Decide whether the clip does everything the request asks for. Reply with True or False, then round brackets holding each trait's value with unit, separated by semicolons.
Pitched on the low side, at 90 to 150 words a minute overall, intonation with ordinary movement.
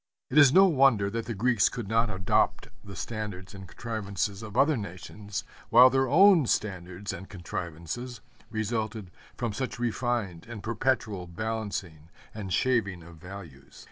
True (105 Hz; 145 wpm; 4.2 semitones)